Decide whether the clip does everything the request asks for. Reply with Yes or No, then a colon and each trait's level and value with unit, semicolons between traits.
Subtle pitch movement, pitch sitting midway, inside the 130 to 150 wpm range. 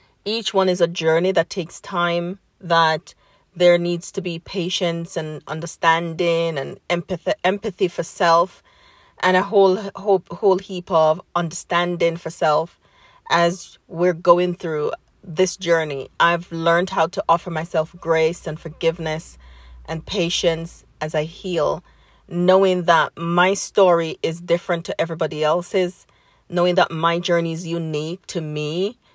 Yes: narrow, 2.0 semitones; medium, 170 Hz; average, 140 wpm